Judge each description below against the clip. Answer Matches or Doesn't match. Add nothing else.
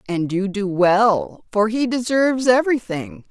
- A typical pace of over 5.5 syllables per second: Doesn't match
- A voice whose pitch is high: Matches